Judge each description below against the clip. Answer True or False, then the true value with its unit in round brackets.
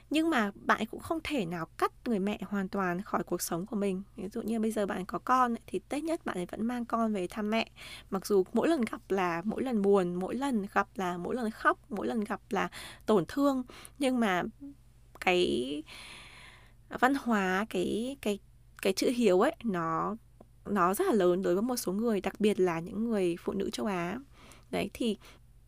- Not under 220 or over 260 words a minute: False (210 wpm)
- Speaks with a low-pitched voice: False (200 Hz)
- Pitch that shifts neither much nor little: True (4.4 semitones)